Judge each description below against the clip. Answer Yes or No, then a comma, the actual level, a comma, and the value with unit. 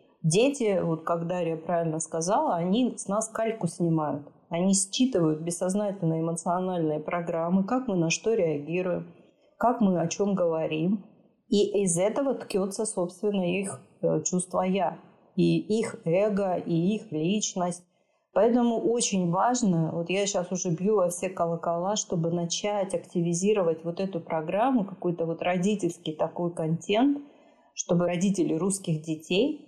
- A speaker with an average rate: Yes, average, 135 wpm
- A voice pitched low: No, medium, 180 Hz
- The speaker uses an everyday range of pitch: Yes, average, 3.6 semitones